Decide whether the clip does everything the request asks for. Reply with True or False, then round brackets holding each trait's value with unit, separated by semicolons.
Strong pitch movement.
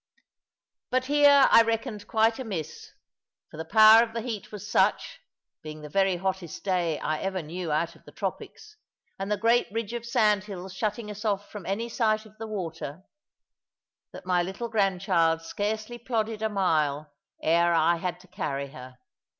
False (4.6 semitones)